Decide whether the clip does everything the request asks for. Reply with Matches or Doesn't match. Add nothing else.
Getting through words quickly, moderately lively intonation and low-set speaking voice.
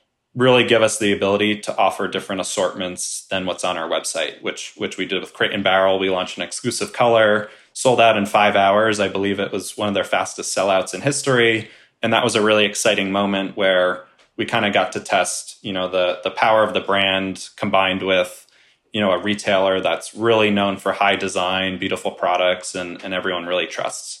Doesn't match